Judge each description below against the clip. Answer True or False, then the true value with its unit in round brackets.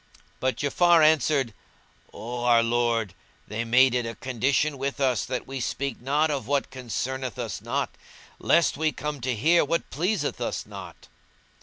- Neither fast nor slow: True (160 wpm)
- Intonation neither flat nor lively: True (3.6 semitones)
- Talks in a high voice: False (130 Hz)